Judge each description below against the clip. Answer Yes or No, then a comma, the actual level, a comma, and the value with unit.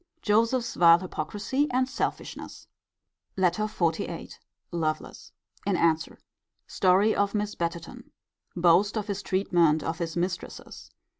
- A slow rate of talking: Yes, slow, 115 wpm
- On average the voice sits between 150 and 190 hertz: Yes, medium, 185 Hz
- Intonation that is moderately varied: Yes, average, 3.7 semitones